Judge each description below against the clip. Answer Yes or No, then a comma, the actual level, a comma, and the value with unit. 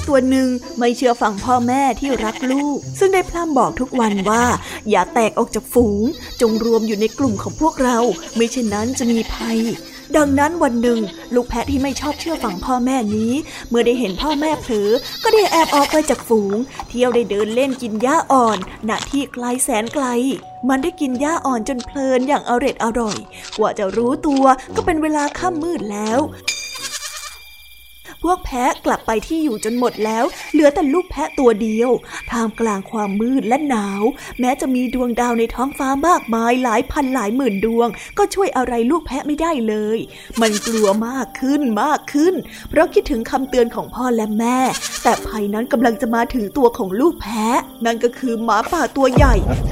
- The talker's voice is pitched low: No, very high, 250 Hz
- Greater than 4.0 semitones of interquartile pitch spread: No, average, 3.7 semitones